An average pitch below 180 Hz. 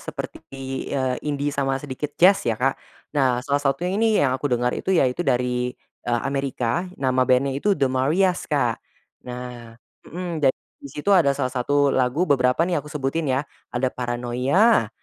Yes: low, 135 Hz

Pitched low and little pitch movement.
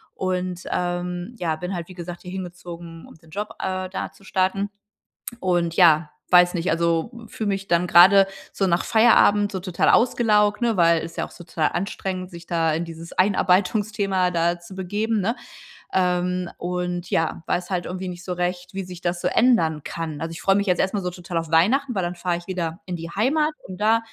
No: medium, 180 Hz; narrow, 2.2 semitones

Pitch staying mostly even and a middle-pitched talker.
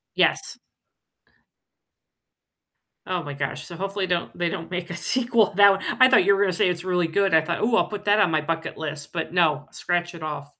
No: average, 3.4 semitones; medium, 175 Hz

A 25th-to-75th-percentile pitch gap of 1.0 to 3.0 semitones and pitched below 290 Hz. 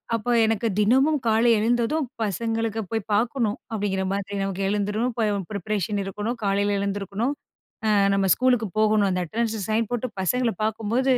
Yes: narrow, 2.5 semitones; high, 215 Hz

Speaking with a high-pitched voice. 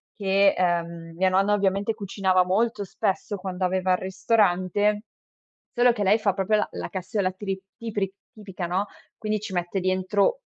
Yes: high, 195 Hz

